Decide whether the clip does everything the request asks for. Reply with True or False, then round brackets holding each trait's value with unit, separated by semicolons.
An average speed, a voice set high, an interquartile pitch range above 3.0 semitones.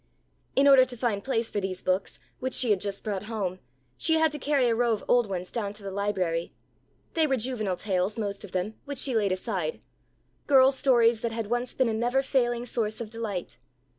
False (215 wpm; 225 Hz; 3.9 semitones)